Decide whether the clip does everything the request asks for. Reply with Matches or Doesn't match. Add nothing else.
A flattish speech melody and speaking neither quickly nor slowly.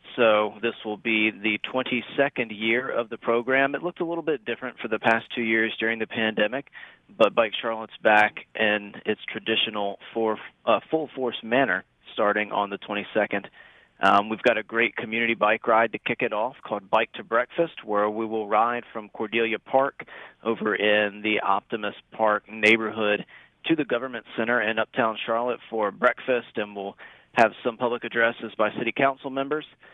Matches